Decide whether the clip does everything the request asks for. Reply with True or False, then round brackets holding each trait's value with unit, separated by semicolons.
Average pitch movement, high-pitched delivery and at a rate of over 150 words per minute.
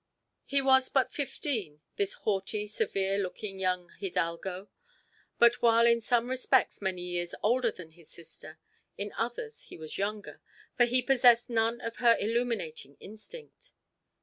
False (4.5 semitones; 220 Hz; 145 wpm)